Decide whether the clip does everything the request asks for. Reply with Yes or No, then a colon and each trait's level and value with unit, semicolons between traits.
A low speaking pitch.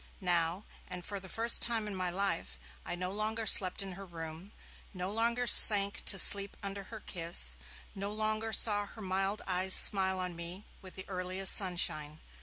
No: high, 195 Hz